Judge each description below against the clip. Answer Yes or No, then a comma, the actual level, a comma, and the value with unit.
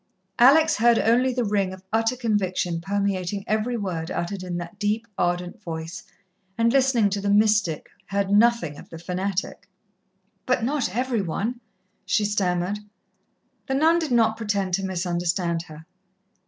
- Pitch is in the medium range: No, high, 200 Hz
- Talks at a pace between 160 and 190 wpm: No, average, 150 wpm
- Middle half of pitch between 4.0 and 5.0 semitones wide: Yes, average, 4.4 semitones